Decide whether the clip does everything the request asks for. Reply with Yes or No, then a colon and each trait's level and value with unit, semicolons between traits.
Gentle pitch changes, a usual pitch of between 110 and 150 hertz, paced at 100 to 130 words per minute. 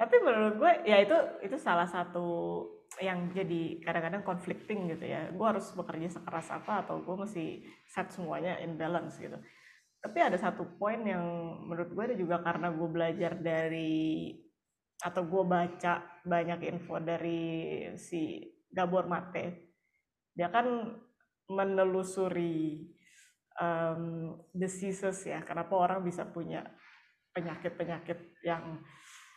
No: narrow, 2.0 semitones; medium, 175 Hz; average, 125 wpm